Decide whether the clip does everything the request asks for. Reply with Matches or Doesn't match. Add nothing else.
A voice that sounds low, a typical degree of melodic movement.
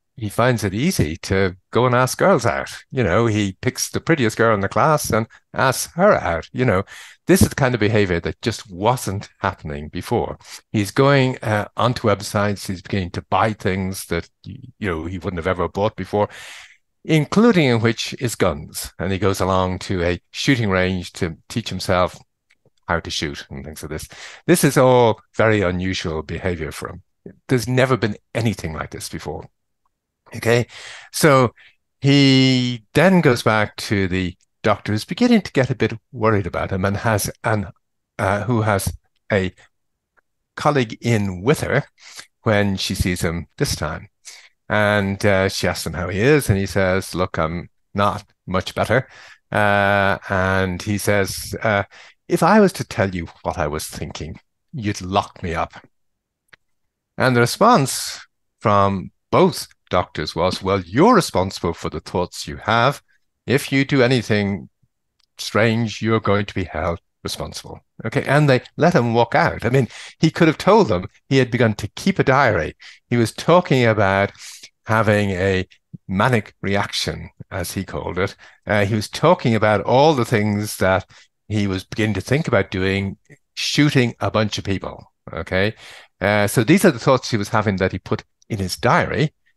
Matches